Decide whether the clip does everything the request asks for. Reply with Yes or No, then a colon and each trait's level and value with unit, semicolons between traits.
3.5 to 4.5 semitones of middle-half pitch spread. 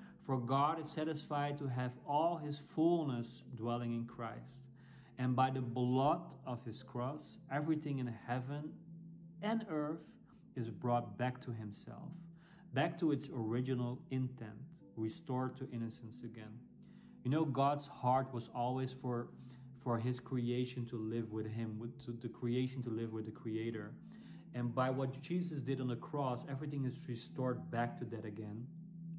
Yes: average, 3.8 semitones